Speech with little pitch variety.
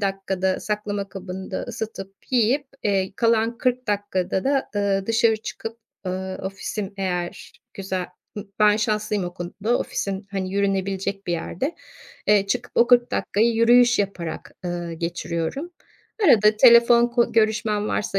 No: average, 3.2 semitones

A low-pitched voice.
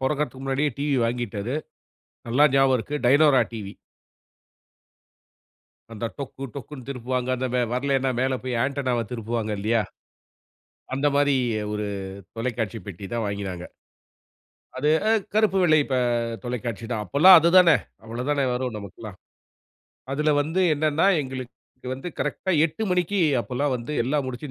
Yes: low, 130 Hz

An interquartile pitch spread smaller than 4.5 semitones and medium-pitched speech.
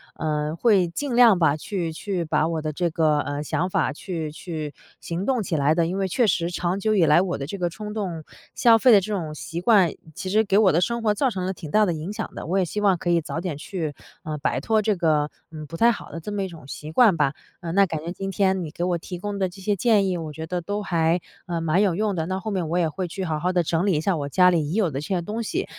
Yes: average, 3.7 semitones; medium, 175 Hz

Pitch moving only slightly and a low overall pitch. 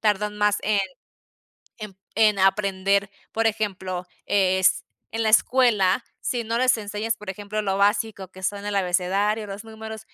No: narrow, 2.1 semitones; high, 205 Hz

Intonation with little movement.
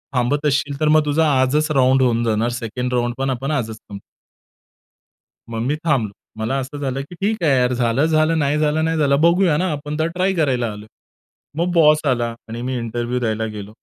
No: average, 4.2 semitones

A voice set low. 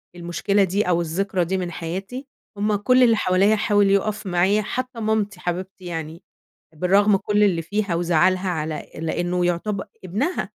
No: high, 190 Hz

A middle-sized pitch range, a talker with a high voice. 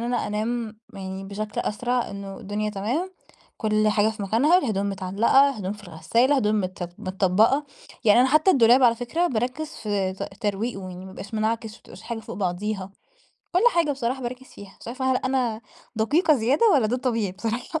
Yes: average, 4.1 semitones; high, 220 Hz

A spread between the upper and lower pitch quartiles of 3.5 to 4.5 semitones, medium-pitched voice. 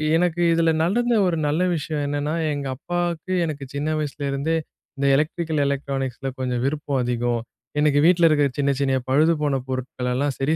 No: average, 3.0 semitones; medium, 145 Hz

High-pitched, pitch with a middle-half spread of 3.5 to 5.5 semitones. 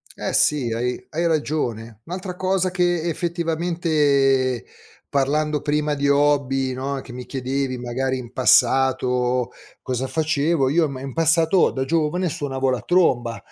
No: medium, 140 Hz; average, 3.9 semitones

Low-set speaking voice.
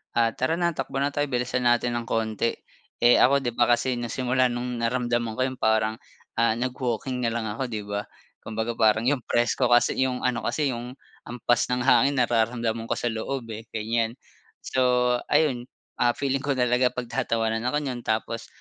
Yes: low, 120 Hz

